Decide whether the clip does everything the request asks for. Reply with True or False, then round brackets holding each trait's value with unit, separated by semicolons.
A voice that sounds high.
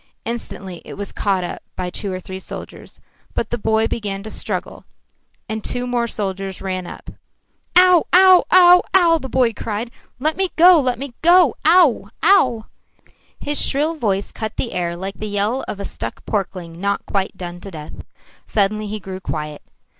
True (215 Hz)